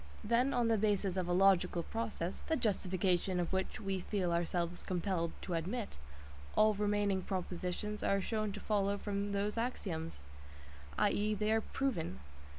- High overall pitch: Yes, high, 200 Hz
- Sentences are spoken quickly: No, average, 155 wpm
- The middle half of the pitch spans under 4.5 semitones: Yes, average, 2.9 semitones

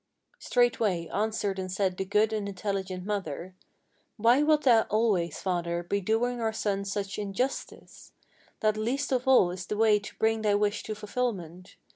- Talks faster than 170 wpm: No, average, 165 wpm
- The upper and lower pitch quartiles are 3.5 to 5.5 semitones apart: No, average, 2.8 semitones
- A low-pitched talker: No, high, 210 Hz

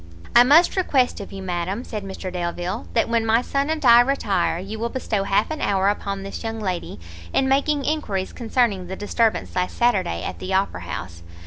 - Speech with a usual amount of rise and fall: Yes, average, 4.6 semitones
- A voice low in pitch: No, high, 205 Hz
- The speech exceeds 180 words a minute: Yes, average, 200 wpm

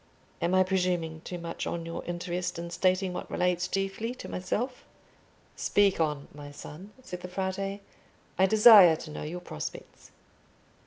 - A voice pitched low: No, medium, 180 Hz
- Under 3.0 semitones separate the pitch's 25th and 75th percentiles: Yes, narrow, 2.4 semitones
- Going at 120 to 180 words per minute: Yes, average, 155 wpm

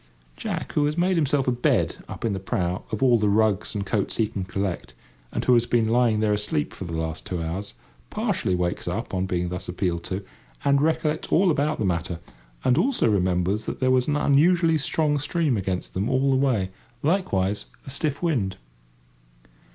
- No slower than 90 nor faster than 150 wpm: No, average, 195 wpm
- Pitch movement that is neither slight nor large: No, wide, 7.2 semitones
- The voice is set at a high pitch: No, low, 110 Hz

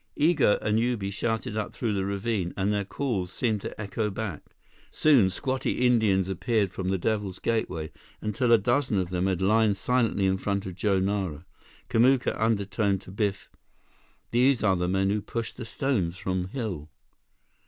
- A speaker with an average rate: Yes, average, 165 wpm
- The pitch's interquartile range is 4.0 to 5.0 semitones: No, average, 3.2 semitones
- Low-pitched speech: Yes, low, 100 Hz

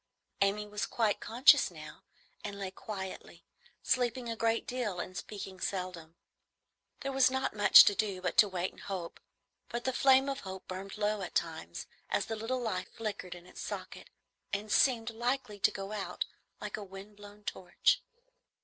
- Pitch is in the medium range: No, high, 210 Hz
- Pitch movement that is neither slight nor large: Yes, average, 3.5 semitones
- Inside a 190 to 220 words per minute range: No, average, 175 wpm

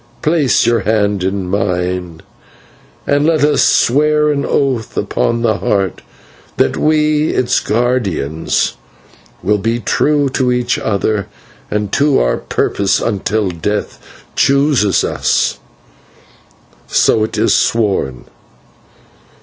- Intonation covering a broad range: Yes, wide, 6.0 semitones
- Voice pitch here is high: No, low, 110 Hz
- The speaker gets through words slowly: Yes, slow, 110 wpm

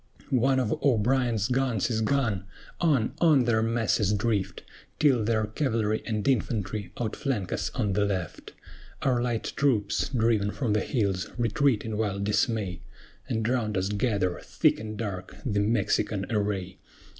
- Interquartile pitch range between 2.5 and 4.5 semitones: Yes, average, 3.1 semitones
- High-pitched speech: No, low, 110 Hz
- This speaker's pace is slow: No, average, 145 wpm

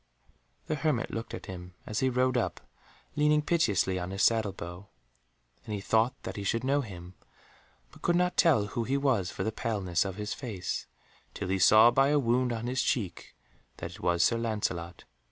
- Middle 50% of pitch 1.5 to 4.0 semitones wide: No, average, 5.2 semitones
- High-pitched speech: No, low, 110 Hz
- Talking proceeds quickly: No, average, 195 wpm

